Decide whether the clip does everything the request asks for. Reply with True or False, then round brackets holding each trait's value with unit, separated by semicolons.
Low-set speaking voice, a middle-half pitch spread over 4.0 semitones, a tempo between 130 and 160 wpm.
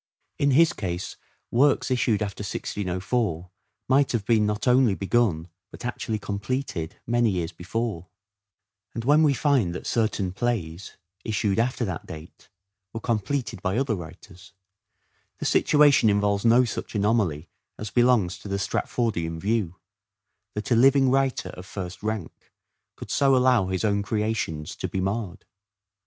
True (105 Hz; 4.6 semitones; 145 wpm)